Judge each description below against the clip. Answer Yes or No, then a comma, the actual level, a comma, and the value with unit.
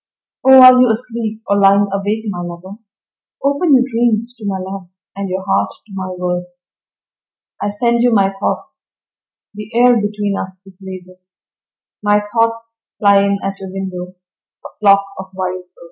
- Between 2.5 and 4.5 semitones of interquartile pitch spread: Yes, average, 3.4 semitones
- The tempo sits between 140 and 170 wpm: Yes, average, 165 wpm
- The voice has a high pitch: Yes, high, 200 Hz